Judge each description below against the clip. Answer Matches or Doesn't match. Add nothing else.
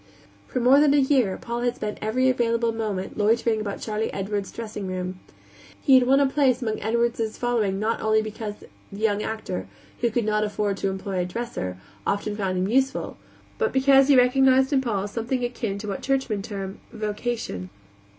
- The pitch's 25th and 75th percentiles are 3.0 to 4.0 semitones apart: Matches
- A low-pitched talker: Doesn't match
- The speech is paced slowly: Doesn't match